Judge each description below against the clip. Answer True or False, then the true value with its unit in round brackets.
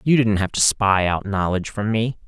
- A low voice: True (105 Hz)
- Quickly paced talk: True (240 wpm)